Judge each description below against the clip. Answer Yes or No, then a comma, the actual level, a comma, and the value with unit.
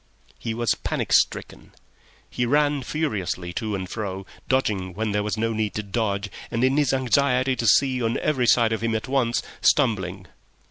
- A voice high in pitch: No, low, 115 Hz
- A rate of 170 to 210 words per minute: Yes, average, 180 wpm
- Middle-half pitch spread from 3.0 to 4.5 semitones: Yes, average, 4.0 semitones